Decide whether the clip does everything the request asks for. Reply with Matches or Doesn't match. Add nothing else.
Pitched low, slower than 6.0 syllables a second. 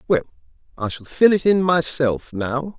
Doesn't match